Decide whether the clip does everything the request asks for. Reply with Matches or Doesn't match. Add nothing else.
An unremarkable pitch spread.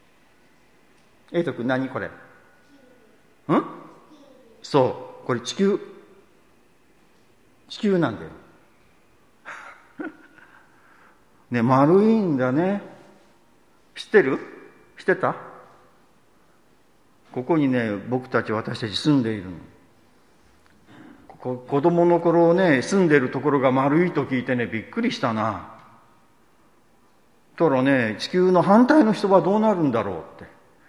Doesn't match